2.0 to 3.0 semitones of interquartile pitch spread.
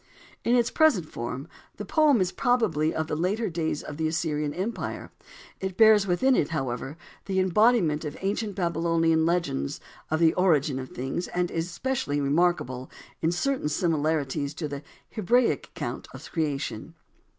No: average, 4.6 semitones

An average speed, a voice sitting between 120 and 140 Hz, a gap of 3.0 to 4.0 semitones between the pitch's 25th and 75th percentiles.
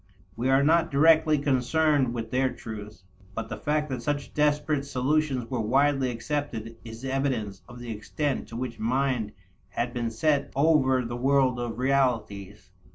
Yes: average, 160 wpm; low, 130 Hz; average, 3.7 semitones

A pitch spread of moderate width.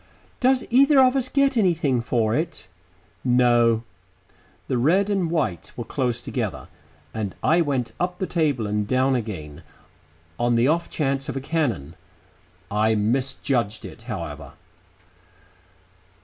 No: wide, 7.1 semitones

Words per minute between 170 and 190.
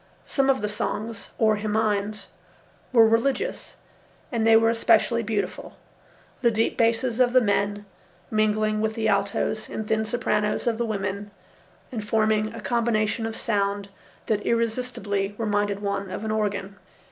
No: average, 145 wpm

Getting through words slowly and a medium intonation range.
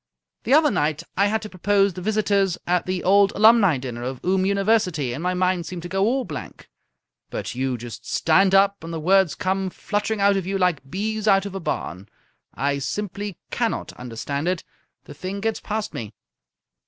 No: average, 190 wpm; average, 4.3 semitones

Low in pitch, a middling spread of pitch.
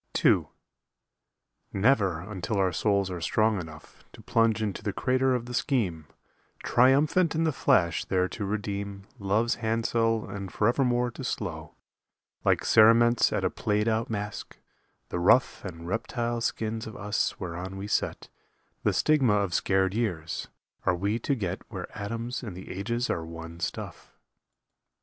Yes: low, 105 Hz; average, 3.7 semitones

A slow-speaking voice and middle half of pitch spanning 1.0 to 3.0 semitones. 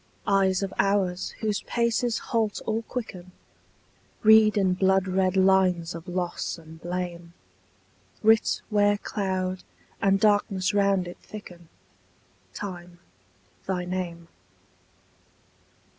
Yes: slow, 100 wpm; narrow, 2.4 semitones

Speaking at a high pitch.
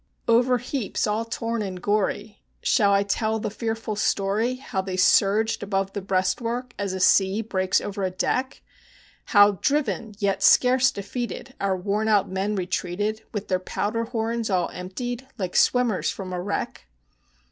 Yes: high, 205 Hz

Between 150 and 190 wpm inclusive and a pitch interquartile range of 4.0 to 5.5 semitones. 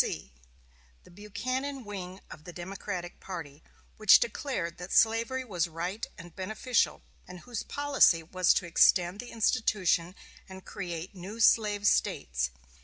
No: slow, 135 wpm; average, 4.3 semitones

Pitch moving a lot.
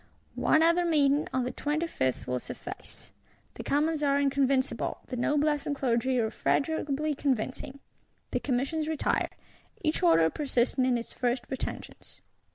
No: average, 3.2 semitones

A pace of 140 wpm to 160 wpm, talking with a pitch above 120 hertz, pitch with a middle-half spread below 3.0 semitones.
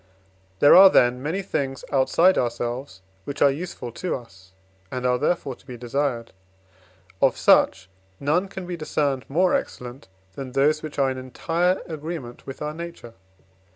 No: average, 155 wpm; medium, 140 Hz; average, 4.9 semitones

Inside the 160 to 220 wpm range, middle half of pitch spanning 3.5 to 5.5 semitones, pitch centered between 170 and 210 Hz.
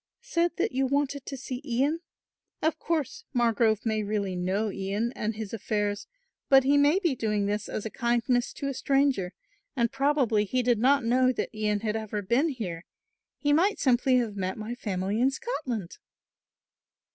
No: average, 175 wpm; average, 4.6 semitones; high, 240 Hz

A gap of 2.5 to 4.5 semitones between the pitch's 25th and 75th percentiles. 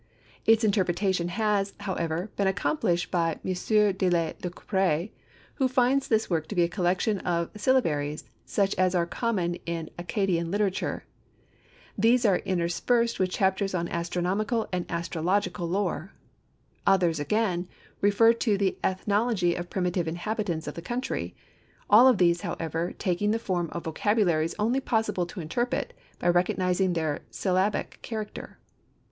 Yes: average, 3.4 semitones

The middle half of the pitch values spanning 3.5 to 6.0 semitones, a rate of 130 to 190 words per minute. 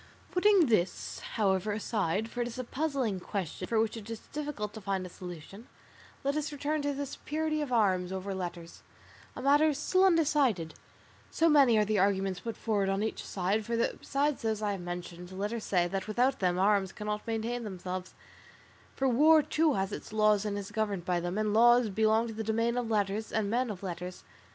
No: average, 4.6 semitones; average, 200 wpm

